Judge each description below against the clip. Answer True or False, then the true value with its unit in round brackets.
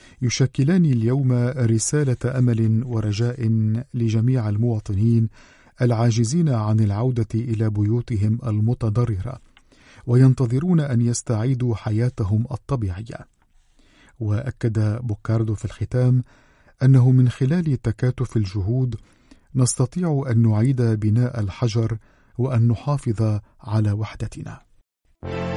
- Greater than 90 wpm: False (85 wpm)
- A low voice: True (120 Hz)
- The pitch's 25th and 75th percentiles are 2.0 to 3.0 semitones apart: True (2.4 semitones)